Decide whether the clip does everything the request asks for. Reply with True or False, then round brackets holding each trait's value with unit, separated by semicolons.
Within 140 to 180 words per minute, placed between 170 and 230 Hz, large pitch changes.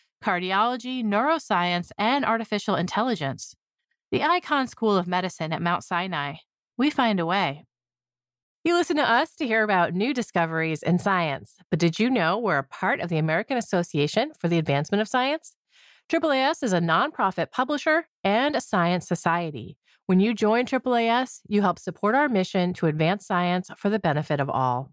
True (170 wpm; 190 Hz; 6.1 semitones)